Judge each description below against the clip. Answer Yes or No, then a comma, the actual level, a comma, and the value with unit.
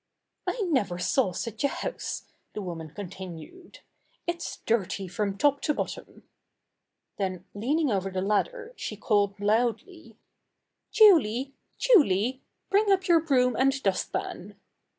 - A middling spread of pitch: No, wide, 8.9 semitones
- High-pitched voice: Yes, high, 235 Hz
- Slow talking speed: Yes, slow, 130 wpm